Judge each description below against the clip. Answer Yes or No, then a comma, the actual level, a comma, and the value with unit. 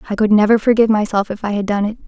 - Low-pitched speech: No, high, 210 Hz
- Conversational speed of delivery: No, fast, 290 wpm